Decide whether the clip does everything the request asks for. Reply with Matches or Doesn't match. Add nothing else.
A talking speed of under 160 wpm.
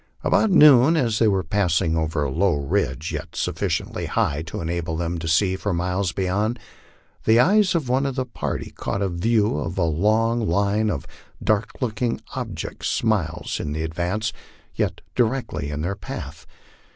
Doesn't match